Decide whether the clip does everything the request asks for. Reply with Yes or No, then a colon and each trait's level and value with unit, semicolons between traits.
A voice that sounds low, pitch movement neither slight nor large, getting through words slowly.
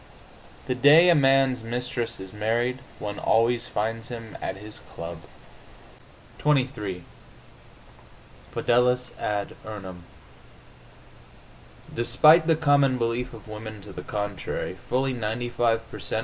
Yes: low, 120 Hz; average, 3.1 semitones; slow, 115 wpm